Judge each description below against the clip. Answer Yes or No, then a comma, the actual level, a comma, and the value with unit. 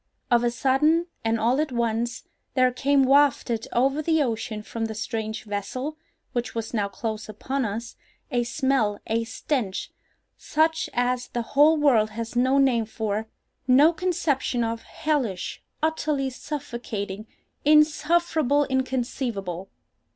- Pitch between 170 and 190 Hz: No, high, 245 Hz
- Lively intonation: No, average, 4.2 semitones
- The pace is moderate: No, slow, 120 wpm